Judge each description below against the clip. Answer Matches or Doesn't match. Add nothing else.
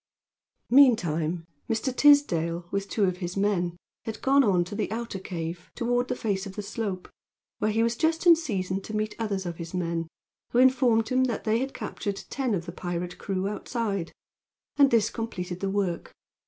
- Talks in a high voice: Matches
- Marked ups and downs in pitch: Doesn't match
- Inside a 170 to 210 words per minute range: Matches